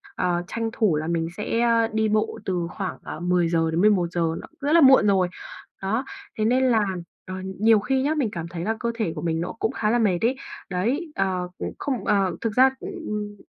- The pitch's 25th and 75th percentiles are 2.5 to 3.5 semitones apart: No, average, 4.7 semitones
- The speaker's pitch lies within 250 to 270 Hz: No, high, 210 Hz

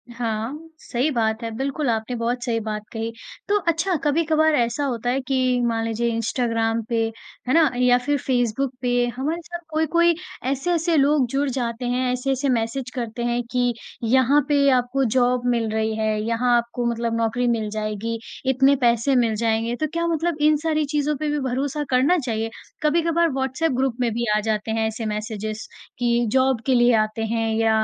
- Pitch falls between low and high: No, high, 245 Hz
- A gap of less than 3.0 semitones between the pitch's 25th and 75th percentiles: No, average, 3.5 semitones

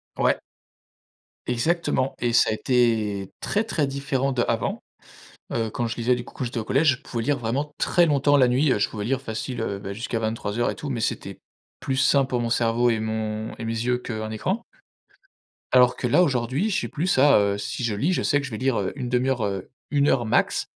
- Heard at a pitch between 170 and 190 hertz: No, low, 125 Hz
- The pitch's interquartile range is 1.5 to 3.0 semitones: No, average, 3.5 semitones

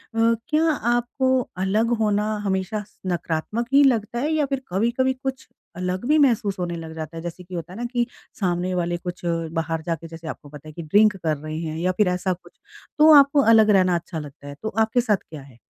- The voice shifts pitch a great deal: Yes, wide, 5.8 semitones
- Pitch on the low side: No, medium, 185 Hz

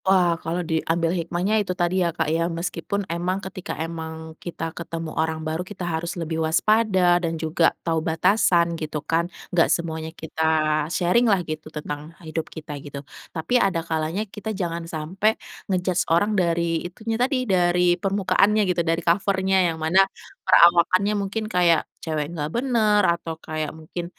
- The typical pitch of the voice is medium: Yes, medium, 170 Hz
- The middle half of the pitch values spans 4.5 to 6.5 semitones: No, average, 2.7 semitones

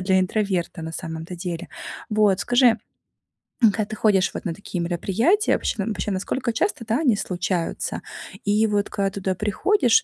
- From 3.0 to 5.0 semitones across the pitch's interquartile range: Yes, average, 3.4 semitones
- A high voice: Yes, high, 200 Hz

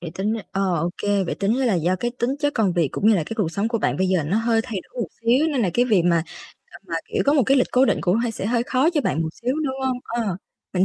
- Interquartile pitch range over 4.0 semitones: Yes, average, 5.0 semitones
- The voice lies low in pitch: No, high, 225 Hz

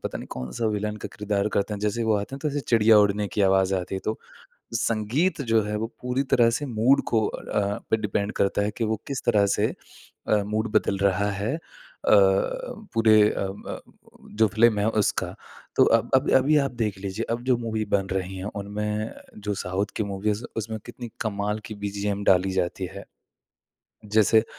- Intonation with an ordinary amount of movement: No, narrow, 2.1 semitones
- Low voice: Yes, low, 105 Hz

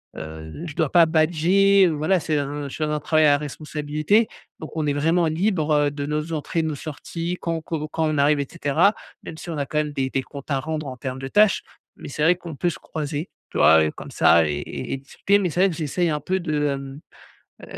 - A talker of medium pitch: Yes, medium, 155 Hz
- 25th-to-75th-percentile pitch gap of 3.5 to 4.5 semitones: No, average, 2.8 semitones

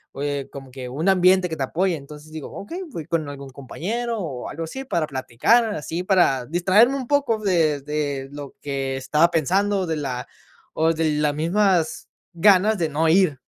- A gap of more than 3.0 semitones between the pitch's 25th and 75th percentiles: Yes, average, 5.0 semitones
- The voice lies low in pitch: No, medium, 160 Hz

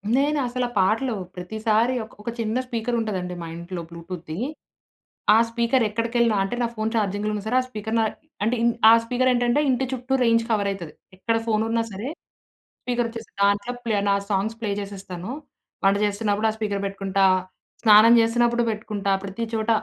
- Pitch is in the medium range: No, high, 220 Hz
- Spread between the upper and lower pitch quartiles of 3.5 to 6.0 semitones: No, average, 3.0 semitones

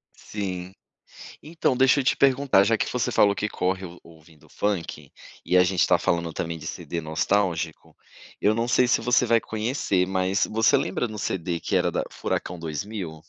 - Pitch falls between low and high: No, very low, 95 Hz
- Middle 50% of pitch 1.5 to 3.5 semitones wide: No, average, 4.8 semitones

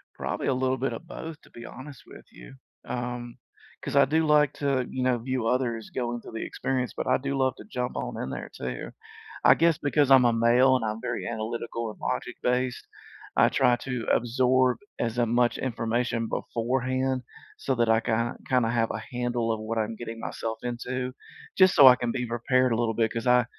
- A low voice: Yes, low, 125 Hz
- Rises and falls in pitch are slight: Yes, narrow, 2.0 semitones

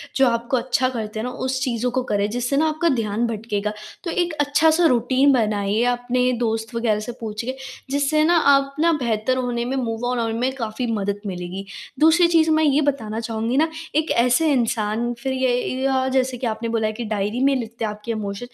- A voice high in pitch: Yes, high, 245 Hz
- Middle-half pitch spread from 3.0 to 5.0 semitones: Yes, average, 3.4 semitones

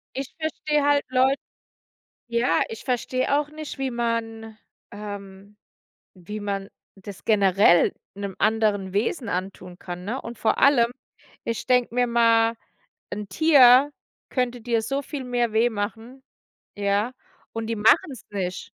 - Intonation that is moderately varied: Yes, average, 3.7 semitones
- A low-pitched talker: No, high, 230 Hz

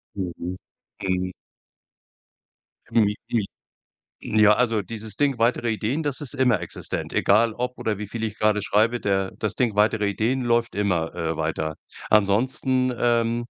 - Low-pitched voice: Yes, low, 110 Hz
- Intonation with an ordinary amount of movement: Yes, average, 3.1 semitones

